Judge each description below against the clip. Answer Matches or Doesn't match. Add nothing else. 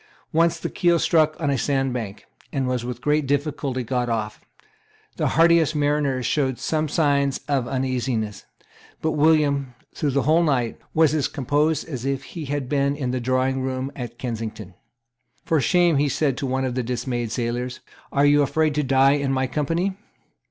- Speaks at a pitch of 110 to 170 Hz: Matches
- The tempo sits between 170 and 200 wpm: Matches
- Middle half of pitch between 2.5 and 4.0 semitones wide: Matches